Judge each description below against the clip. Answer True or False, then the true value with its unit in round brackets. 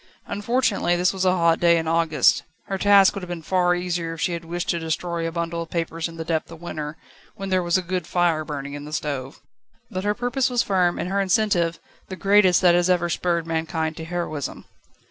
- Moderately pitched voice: True (175 Hz)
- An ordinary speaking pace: False (225 wpm)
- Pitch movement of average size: False (2.2 semitones)